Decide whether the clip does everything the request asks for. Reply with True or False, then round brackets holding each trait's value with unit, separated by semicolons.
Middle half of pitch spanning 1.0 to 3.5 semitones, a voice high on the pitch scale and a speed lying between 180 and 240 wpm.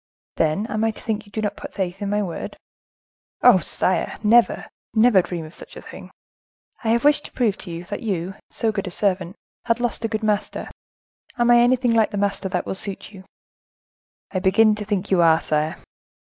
True (3.2 semitones; 205 Hz; 205 wpm)